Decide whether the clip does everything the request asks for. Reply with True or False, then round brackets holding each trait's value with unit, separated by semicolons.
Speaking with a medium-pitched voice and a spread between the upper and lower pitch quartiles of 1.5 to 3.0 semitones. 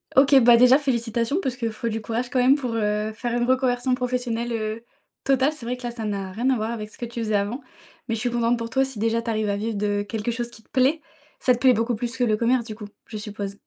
False (235 Hz; 2.5 semitones)